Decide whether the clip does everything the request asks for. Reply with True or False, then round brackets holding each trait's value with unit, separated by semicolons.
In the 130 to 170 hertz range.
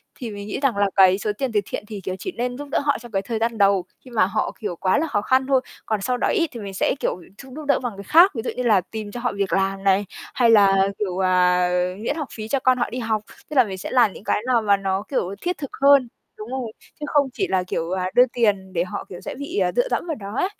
False (220 Hz)